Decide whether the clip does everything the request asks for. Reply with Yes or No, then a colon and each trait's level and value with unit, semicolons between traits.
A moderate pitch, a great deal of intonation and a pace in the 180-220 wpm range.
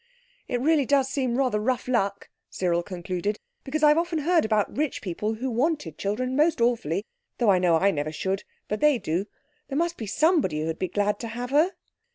No: high, 235 Hz; wide, 6.6 semitones; average, 190 wpm